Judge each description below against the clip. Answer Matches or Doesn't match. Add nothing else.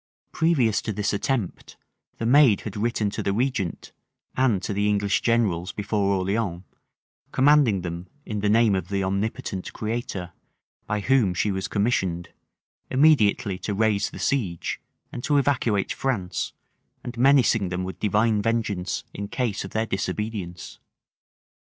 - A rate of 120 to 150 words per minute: Matches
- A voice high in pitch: Doesn't match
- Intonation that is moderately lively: Matches